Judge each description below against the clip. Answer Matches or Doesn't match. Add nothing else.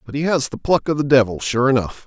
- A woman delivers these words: Doesn't match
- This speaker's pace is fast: Matches